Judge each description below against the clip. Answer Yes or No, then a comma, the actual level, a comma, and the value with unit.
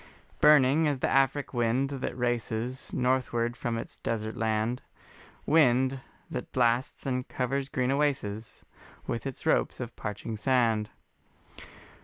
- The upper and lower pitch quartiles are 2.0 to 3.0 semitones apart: Yes, average, 2.7 semitones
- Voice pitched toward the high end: No, low, 125 Hz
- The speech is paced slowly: Yes, slow, 125 wpm